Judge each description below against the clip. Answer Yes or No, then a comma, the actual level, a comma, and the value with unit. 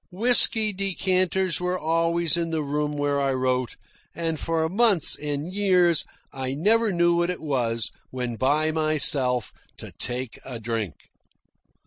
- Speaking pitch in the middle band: Yes, medium, 160 Hz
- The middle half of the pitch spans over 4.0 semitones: Yes, average, 5.2 semitones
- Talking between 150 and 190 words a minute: No, average, 140 wpm